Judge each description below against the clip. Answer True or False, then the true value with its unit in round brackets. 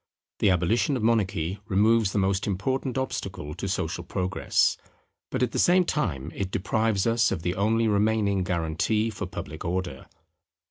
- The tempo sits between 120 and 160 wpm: True (155 wpm)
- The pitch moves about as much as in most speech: True (3.6 semitones)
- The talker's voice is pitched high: False (100 Hz)